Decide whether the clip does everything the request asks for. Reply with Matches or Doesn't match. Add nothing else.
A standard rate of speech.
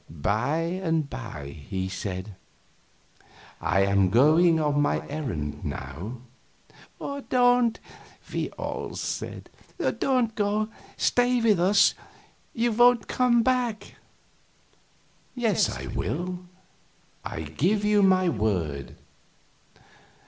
Doesn't match